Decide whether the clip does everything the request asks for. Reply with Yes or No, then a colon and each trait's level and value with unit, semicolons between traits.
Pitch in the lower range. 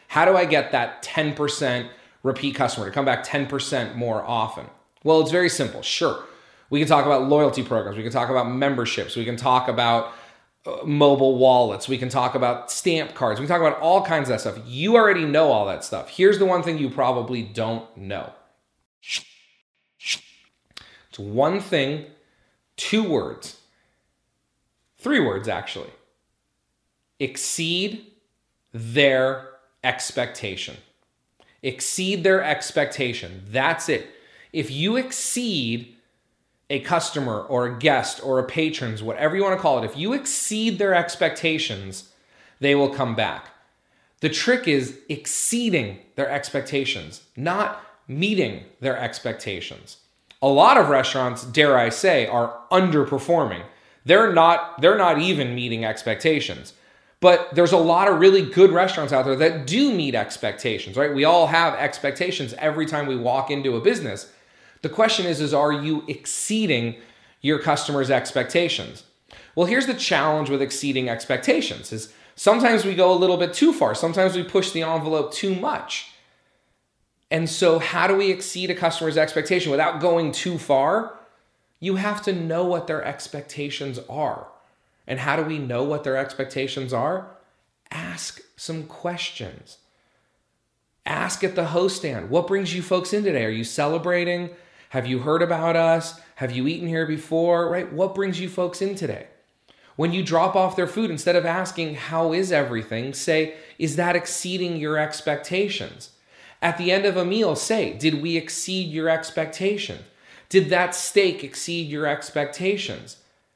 No: medium, 155 Hz